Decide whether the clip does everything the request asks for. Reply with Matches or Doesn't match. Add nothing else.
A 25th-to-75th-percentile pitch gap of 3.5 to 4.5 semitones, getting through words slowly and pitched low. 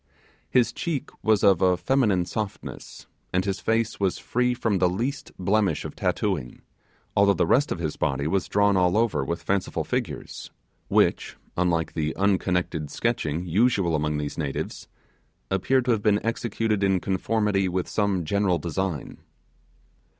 Doesn't match